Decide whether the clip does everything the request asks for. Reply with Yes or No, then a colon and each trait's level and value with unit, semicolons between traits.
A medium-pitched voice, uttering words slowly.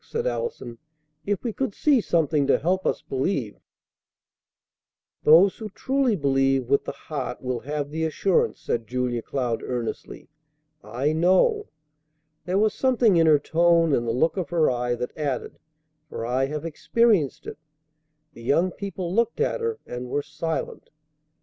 No: medium, 155 Hz; average, 160 wpm